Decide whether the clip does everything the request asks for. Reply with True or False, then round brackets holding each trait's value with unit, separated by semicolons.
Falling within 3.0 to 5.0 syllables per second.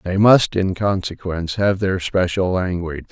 True (4.7 syllables/s)